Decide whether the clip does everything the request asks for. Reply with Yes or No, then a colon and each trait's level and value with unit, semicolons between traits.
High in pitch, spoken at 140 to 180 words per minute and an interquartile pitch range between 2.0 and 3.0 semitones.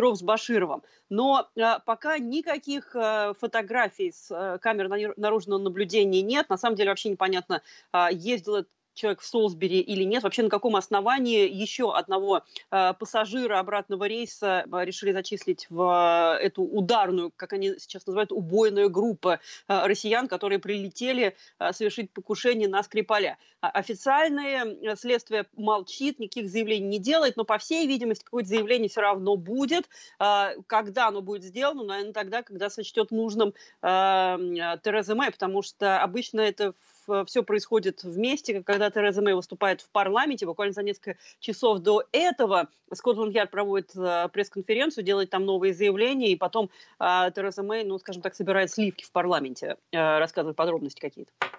Yes: high, 205 Hz; average, 150 wpm; average, 2.7 semitones